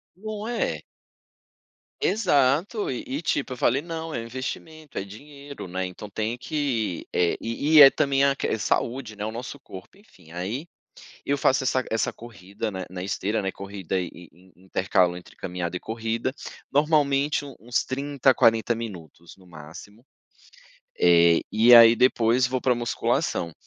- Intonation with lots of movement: Yes, wide, 6.5 semitones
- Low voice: Yes, low, 115 Hz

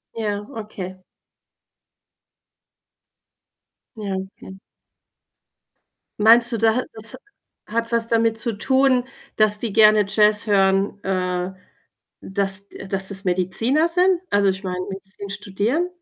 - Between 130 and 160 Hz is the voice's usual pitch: No, high, 210 Hz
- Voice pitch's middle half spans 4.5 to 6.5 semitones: No, average, 2.9 semitones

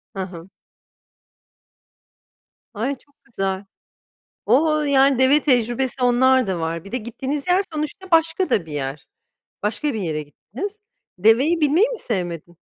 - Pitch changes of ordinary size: No, wide, 7.7 semitones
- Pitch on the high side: Yes, very high, 250 Hz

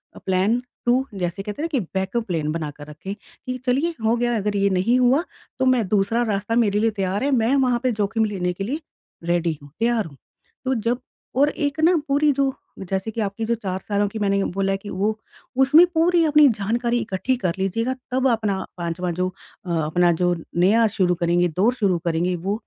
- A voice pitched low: No, high, 205 Hz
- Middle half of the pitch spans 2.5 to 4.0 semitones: No, average, 4.8 semitones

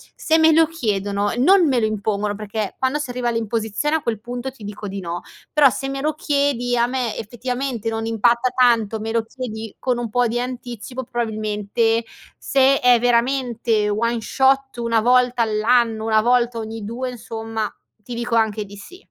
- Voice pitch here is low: No, high, 235 Hz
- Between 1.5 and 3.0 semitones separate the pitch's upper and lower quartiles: Yes, narrow, 2.6 semitones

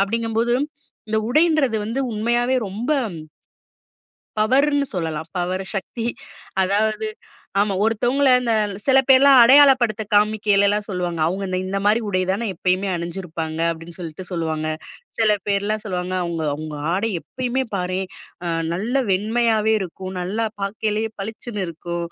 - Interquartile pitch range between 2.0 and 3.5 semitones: No, average, 4.2 semitones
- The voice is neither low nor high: No, high, 210 Hz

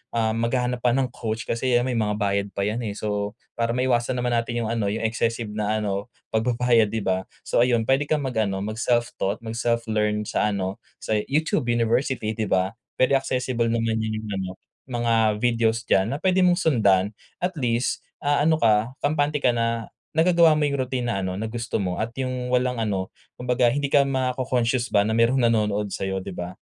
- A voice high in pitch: No, low, 115 Hz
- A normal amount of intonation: Yes, average, 3.0 semitones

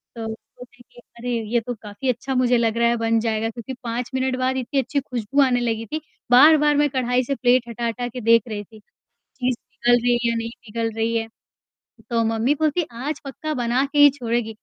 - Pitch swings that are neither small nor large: No, narrow, 2.3 semitones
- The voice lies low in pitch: No, high, 245 Hz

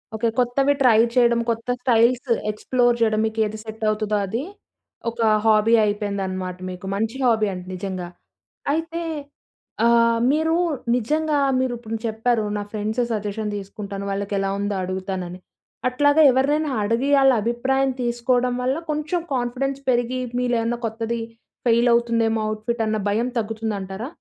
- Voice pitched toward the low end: No, high, 230 Hz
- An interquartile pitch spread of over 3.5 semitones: No, average, 3.0 semitones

